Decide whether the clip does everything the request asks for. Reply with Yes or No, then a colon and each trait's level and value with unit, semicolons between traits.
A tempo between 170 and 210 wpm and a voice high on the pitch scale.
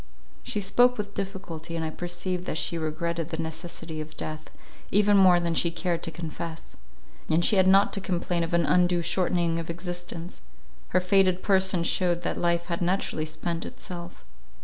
No: average, 175 wpm; medium, 175 Hz